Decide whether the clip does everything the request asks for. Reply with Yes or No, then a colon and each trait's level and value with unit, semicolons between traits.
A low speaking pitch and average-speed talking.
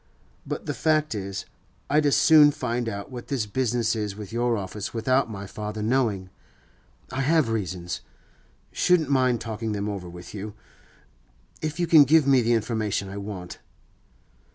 Yes: low, 115 Hz; average, 160 wpm